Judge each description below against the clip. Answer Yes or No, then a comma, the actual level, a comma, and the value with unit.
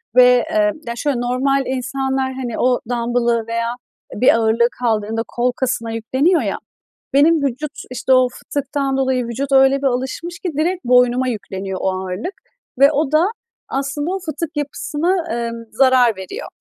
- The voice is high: Yes, very high, 260 Hz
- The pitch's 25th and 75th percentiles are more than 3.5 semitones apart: No, average, 3.1 semitones